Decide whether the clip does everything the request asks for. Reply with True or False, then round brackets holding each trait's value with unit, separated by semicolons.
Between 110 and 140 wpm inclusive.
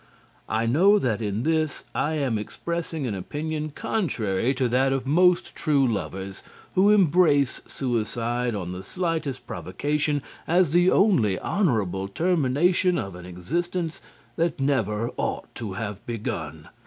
True (135 wpm)